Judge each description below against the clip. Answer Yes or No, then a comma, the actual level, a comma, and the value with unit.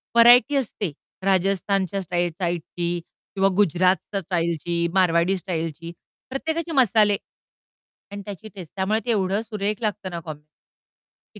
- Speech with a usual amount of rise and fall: Yes, average, 3.5 semitones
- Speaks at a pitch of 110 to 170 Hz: No, high, 190 Hz